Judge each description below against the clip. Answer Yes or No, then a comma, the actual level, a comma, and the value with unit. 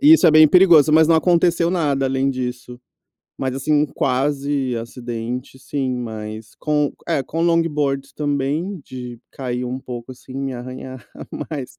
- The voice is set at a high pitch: No, low, 135 Hz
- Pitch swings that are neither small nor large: Yes, average, 3.5 semitones